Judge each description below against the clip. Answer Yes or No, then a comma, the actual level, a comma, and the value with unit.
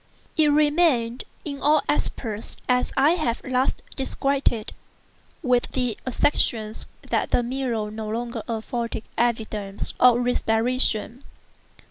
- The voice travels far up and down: No, average, 3.2 semitones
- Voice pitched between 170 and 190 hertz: No, high, 245 Hz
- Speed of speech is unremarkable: No, slow, 115 wpm